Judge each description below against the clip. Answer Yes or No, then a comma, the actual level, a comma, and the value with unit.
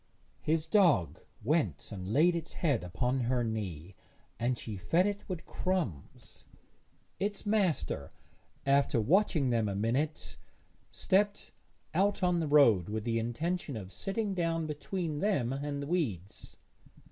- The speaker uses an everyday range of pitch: No, wide, 8.0 semitones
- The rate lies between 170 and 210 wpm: No, slow, 135 wpm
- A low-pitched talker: No, medium, 145 Hz